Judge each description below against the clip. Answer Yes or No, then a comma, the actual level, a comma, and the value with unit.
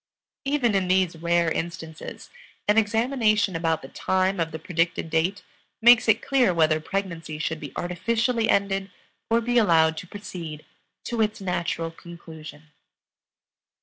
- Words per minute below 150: Yes, average, 140 wpm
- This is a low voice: No, medium, 180 Hz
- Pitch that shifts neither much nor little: Yes, average, 4.7 semitones